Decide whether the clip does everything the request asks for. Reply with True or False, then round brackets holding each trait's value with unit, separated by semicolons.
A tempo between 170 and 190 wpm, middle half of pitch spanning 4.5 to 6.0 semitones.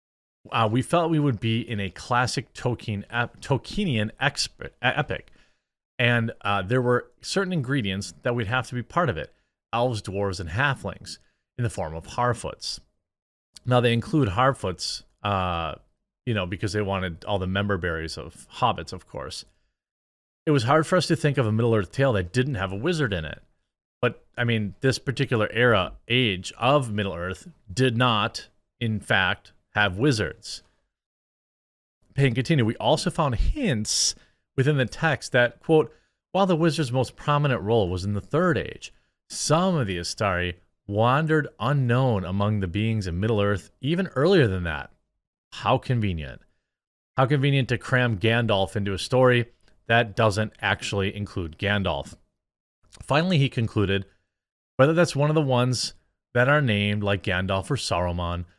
False (160 wpm; 5.1 semitones)